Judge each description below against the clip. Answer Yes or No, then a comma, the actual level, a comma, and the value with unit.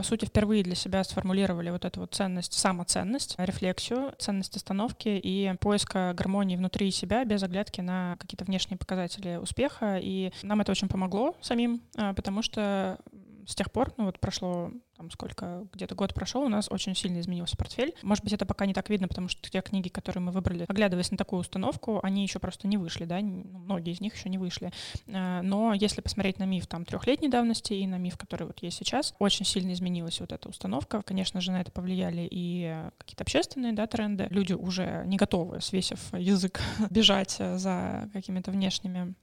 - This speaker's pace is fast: Yes, fast, 190 wpm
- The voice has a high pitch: Yes, high, 195 Hz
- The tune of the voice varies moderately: No, narrow, 2.1 semitones